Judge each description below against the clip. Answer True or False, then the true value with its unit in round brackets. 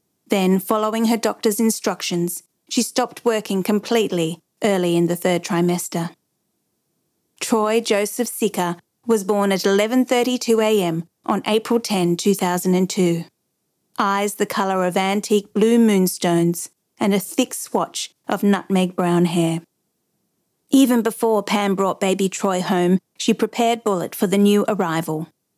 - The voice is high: True (200 Hz)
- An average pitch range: True (3.6 semitones)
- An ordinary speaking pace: False (125 wpm)